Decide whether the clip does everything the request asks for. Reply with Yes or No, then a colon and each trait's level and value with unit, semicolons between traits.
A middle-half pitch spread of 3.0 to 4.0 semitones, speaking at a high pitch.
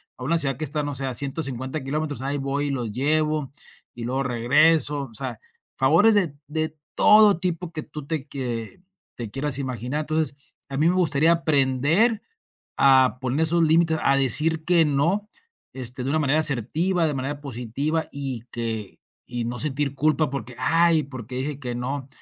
No: average, 3.4 semitones; medium, 145 Hz